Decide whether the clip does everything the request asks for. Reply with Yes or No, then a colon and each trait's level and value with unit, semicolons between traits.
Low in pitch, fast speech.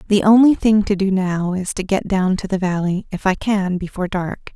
No: high, 190 Hz; fast, 235 wpm